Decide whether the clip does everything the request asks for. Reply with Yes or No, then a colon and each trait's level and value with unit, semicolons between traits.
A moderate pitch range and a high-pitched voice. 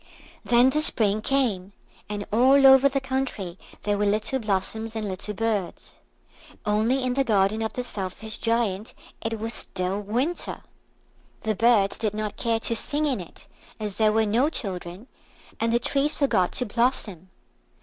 Yes: average, 3.6 semitones; high, 220 Hz